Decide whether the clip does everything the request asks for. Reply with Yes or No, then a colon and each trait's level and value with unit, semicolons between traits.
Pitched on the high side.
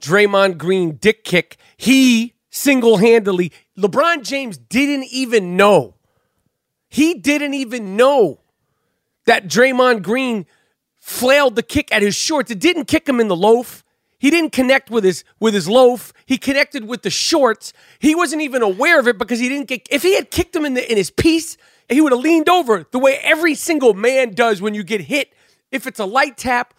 Yes: very high, 250 Hz